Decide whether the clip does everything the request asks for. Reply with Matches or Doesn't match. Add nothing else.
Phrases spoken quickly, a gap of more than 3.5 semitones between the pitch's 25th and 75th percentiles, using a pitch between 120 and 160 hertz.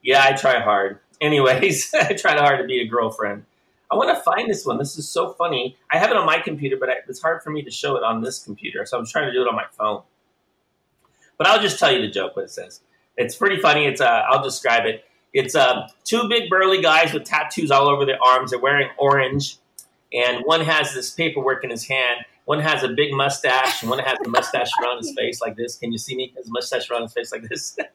Matches